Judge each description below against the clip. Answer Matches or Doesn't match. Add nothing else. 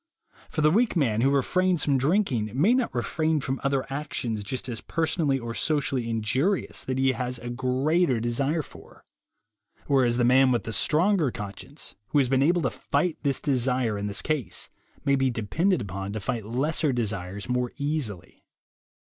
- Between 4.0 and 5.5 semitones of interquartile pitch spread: Matches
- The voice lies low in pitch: Matches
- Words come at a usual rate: Matches